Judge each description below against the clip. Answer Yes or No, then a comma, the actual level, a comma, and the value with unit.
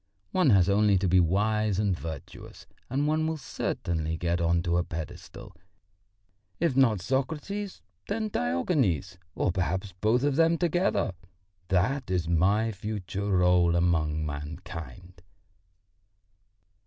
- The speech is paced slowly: Yes, slow, 125 wpm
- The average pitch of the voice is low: Yes, very low, 95 Hz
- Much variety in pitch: Yes, wide, 7.2 semitones